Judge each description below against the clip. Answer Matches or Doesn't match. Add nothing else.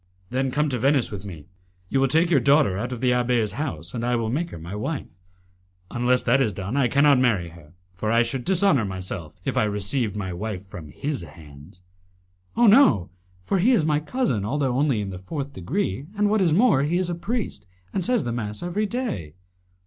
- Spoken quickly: Matches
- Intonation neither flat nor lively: Doesn't match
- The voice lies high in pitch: Doesn't match